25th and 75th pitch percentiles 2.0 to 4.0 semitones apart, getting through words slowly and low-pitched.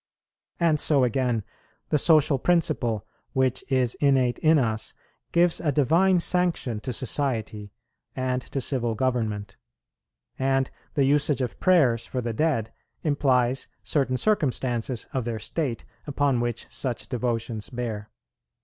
Yes: average, 3.5 semitones; slow, 130 wpm; low, 130 Hz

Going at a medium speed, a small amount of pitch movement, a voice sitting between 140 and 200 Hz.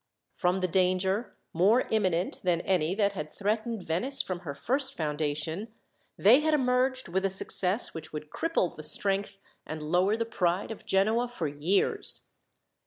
No: average, 160 wpm; average, 4.7 semitones; high, 190 Hz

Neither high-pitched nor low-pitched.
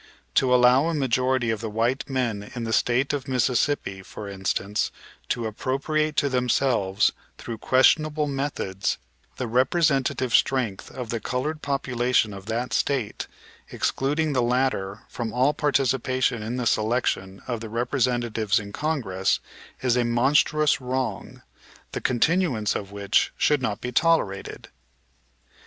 No: low, 125 Hz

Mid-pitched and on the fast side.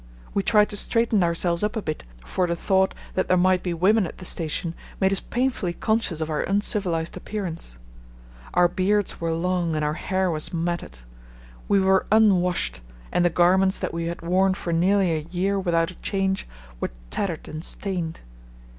No: medium, 180 Hz; average, 180 wpm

